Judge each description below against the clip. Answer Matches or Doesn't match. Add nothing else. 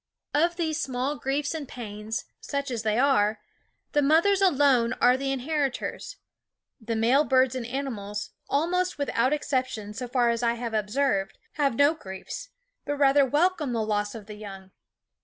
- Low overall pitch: Doesn't match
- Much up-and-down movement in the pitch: Doesn't match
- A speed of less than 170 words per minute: Matches